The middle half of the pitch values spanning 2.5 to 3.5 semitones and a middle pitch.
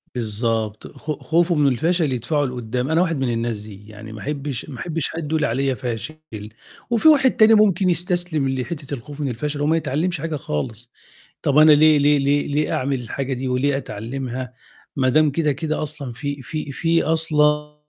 No: average, 3.9 semitones; medium, 145 Hz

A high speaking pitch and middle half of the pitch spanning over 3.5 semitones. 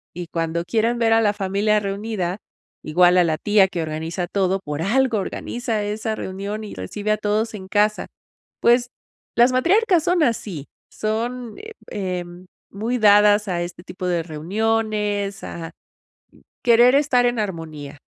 Yes: high, 205 Hz; average, 4.0 semitones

